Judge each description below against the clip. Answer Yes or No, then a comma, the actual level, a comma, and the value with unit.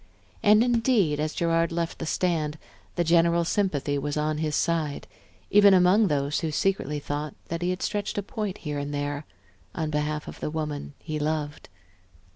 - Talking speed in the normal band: Yes, average, 175 wpm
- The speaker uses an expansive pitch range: No, average, 3.5 semitones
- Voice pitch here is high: No, medium, 160 Hz